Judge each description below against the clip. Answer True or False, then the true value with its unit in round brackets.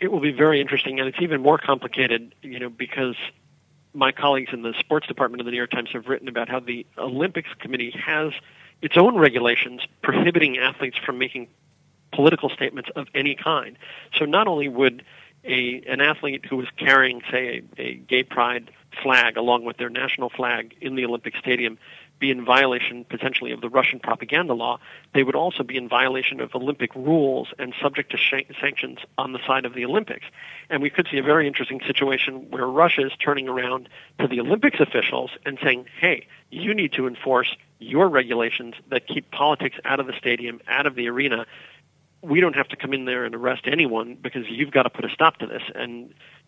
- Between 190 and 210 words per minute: True (200 wpm)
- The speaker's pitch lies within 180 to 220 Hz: False (130 Hz)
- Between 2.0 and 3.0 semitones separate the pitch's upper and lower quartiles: True (2.7 semitones)